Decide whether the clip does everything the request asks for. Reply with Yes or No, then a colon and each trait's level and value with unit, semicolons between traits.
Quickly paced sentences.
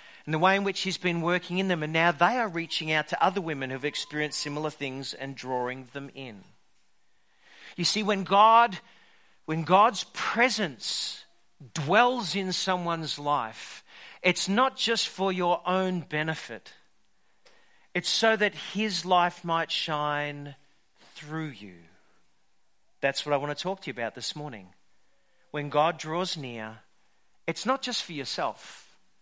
No: average, 150 wpm